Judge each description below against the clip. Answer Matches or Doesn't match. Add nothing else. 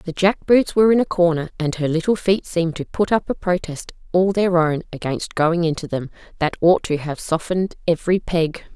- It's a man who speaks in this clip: Doesn't match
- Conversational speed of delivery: Doesn't match